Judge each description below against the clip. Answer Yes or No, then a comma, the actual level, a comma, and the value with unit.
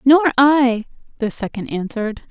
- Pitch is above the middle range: Yes, very high, 250 Hz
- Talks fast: No, slow, 130 wpm